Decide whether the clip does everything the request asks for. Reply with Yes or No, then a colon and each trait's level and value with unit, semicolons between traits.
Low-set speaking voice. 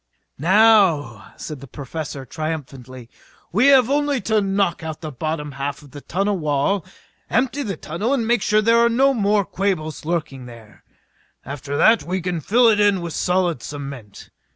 No: medium, 170 Hz